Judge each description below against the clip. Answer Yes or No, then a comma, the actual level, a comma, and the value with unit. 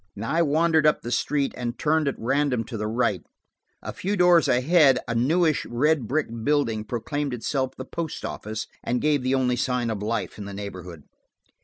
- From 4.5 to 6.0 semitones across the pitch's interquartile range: Yes, average, 4.8 semitones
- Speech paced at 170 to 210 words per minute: Yes, average, 185 wpm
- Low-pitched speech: Yes, low, 130 Hz